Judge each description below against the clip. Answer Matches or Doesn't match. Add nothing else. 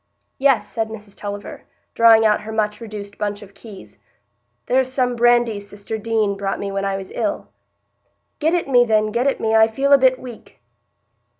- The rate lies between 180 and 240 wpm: Matches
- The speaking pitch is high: Matches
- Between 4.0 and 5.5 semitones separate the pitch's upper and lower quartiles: Doesn't match